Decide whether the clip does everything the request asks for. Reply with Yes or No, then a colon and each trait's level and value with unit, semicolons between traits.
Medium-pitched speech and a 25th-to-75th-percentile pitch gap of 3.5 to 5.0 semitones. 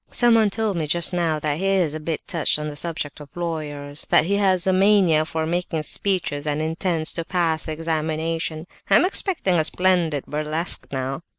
No: medium, 165 Hz; average, 3.1 semitones